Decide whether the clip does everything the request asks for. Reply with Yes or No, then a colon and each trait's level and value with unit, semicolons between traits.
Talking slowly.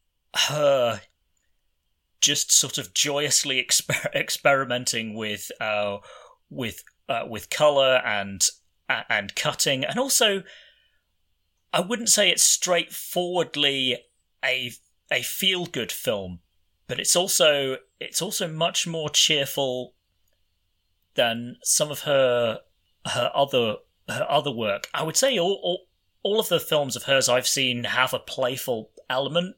Yes: slow, 125 wpm